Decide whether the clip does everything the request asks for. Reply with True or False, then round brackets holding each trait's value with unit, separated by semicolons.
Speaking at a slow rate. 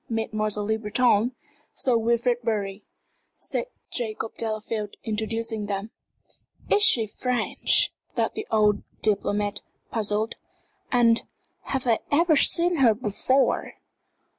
True (110 wpm)